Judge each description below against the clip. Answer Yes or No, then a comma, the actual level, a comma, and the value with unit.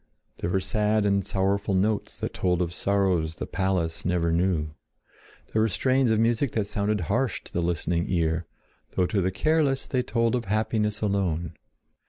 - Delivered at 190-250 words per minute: No, average, 175 wpm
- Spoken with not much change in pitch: No, average, 3.8 semitones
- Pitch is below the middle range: Yes, low, 100 Hz